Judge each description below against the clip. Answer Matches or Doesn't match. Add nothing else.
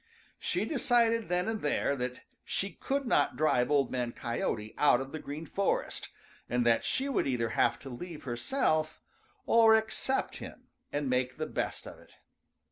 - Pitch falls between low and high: Matches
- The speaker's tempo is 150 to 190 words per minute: Matches